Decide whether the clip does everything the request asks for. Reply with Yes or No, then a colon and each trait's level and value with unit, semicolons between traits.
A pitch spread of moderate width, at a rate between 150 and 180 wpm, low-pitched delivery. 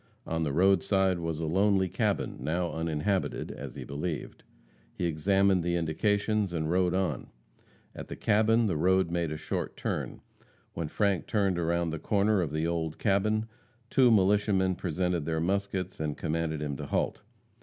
Yes: average, 3.4 semitones; average, 165 wpm; very low, 90 Hz